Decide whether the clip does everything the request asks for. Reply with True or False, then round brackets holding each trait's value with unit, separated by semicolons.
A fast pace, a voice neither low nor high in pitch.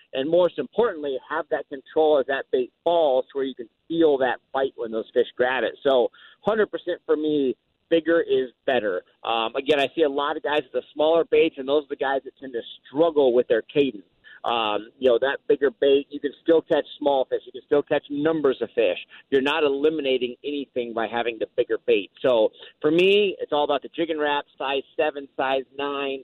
True (215 wpm; 155 Hz)